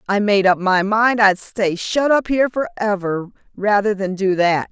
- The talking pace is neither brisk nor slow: Yes, average, 190 wpm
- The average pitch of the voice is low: No, high, 205 Hz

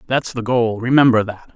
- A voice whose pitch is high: No, low, 120 Hz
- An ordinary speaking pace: Yes, average, 195 wpm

